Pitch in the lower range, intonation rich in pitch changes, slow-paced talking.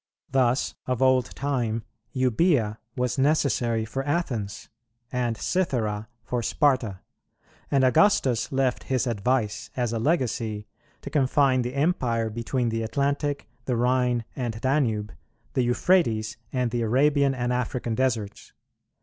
No: low, 125 Hz; average, 3.0 semitones; slow, 125 wpm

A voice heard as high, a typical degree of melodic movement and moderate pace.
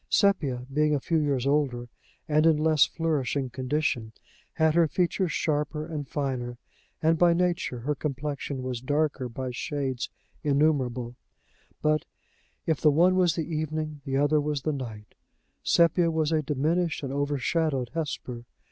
No: medium, 150 Hz; average, 3.1 semitones; average, 145 wpm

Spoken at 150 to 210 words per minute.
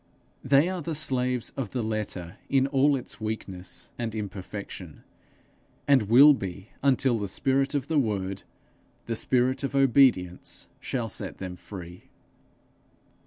No: slow, 135 wpm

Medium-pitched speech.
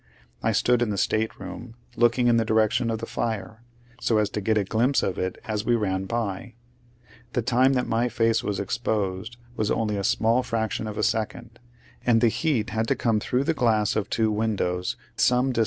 No: low, 110 Hz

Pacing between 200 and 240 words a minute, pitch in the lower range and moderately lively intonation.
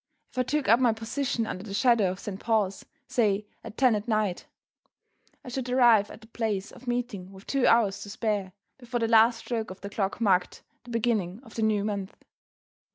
No: fast, 205 wpm; high, 220 Hz; average, 3.1 semitones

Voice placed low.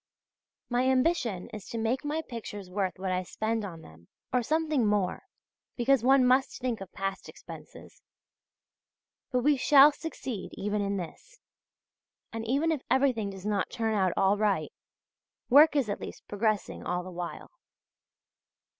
No: high, 225 Hz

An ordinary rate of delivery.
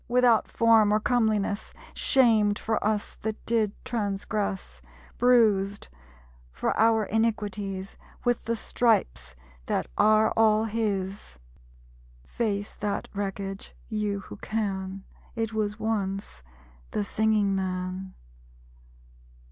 No: slow, 100 wpm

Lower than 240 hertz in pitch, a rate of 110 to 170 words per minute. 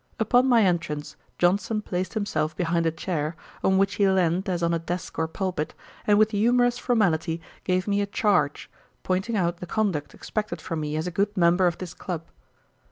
No: medium, 185 Hz; average, 190 wpm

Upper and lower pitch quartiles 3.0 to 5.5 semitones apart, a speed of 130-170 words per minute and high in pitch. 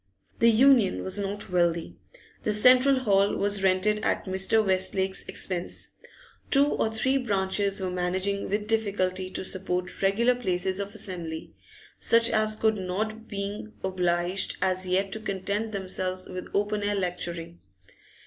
No: narrow, 2.6 semitones; average, 140 wpm; high, 195 Hz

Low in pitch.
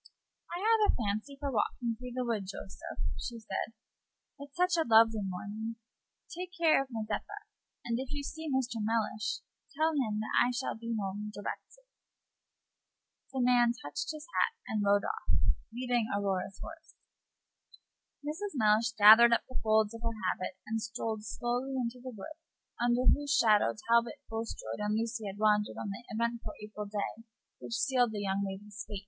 No: high, 230 Hz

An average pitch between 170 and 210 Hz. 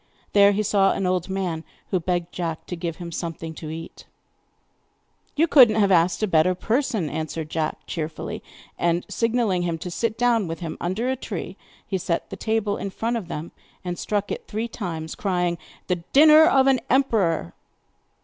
Yes: medium, 185 Hz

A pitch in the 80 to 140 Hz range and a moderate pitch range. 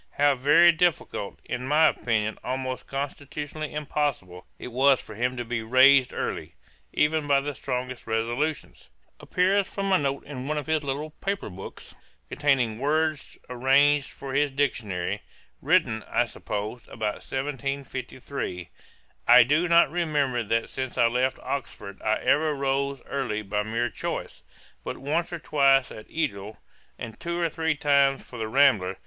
Yes: low, 135 Hz; average, 3.6 semitones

